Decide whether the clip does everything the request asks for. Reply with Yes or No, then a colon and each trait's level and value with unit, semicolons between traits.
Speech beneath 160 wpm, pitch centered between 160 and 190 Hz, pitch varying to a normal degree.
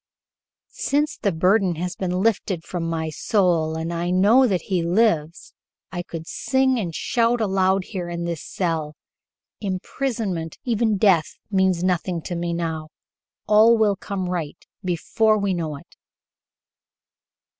Yes: average, 140 wpm; medium, 185 Hz; average, 3.8 semitones